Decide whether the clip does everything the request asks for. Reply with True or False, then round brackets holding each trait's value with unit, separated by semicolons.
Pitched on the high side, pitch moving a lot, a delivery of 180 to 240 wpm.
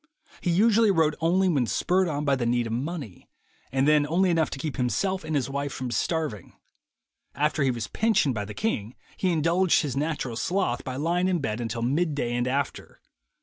False (145 Hz; 5.8 semitones; 200 wpm)